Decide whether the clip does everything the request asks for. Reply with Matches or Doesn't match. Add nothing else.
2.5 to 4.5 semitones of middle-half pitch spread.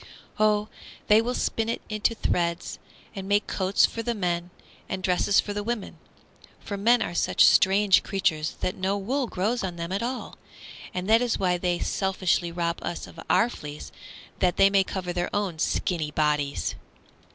Matches